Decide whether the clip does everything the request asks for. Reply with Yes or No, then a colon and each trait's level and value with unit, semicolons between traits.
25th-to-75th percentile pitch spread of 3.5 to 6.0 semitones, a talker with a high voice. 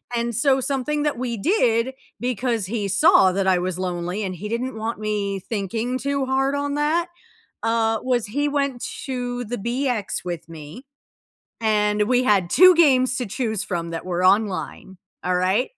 Yes: average, 5.0 semitones; high, 230 Hz